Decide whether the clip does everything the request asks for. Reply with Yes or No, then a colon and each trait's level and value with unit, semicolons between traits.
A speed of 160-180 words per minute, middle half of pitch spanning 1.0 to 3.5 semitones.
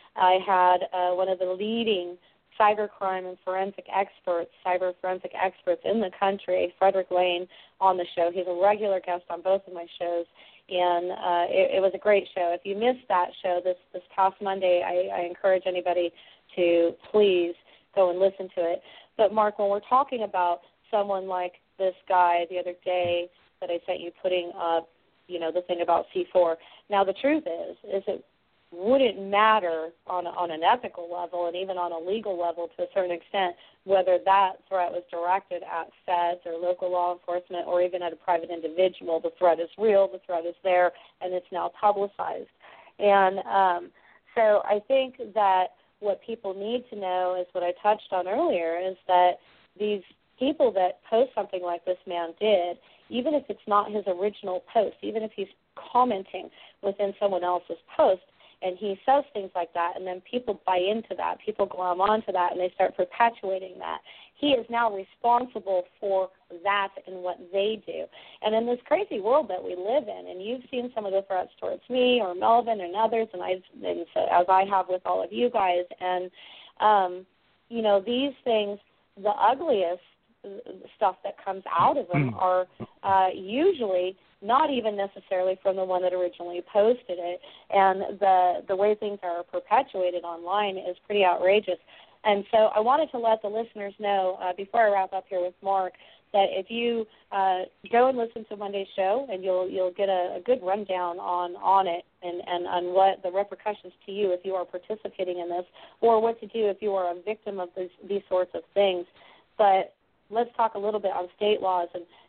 No: average, 190 wpm; narrow, 2.5 semitones